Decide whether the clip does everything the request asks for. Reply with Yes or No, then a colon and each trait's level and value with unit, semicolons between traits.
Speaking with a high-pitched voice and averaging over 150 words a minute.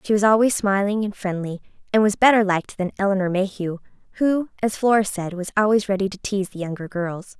Yes: high, 200 Hz; fast, 205 wpm